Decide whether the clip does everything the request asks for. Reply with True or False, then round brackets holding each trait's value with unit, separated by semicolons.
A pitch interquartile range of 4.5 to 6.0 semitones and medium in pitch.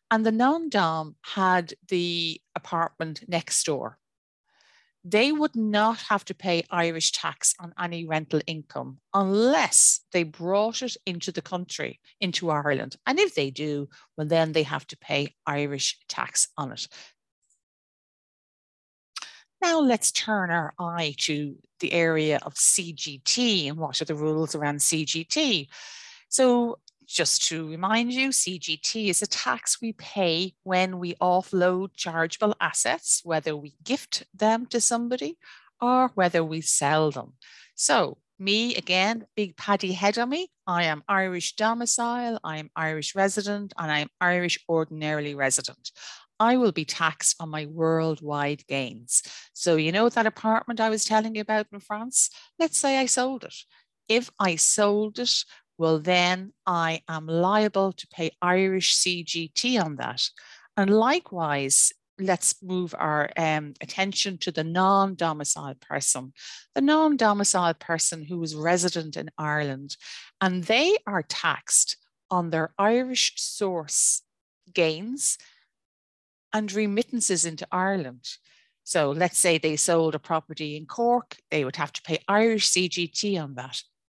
True (5.2 semitones; 180 Hz)